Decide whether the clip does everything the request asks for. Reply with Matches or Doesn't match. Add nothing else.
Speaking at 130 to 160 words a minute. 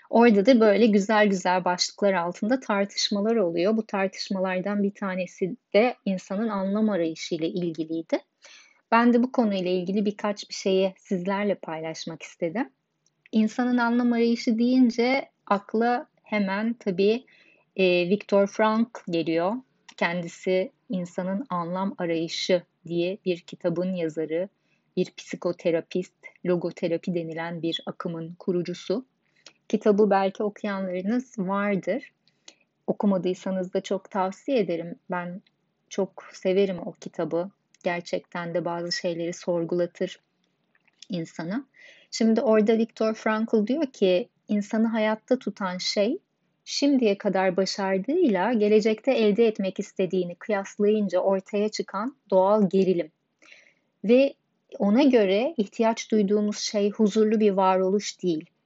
Doesn't match